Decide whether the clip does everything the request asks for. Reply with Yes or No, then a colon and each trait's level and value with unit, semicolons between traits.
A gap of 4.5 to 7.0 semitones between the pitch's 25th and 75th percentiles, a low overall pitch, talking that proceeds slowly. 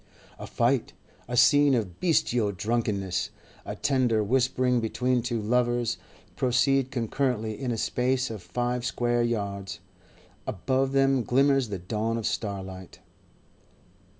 No: average, 3.2 semitones; low, 120 Hz; slow, 125 wpm